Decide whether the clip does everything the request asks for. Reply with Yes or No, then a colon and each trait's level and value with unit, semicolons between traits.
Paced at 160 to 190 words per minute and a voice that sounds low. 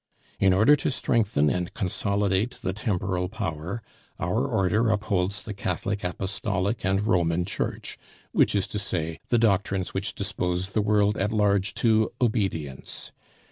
No: average, 140 wpm; low, 100 Hz